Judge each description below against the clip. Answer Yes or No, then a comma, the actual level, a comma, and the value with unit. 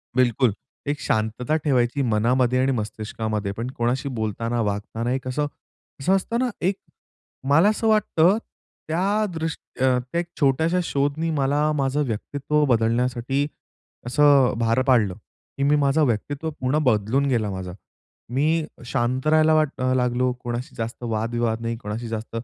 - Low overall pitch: Yes, low, 130 Hz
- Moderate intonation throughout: Yes, average, 4.2 semitones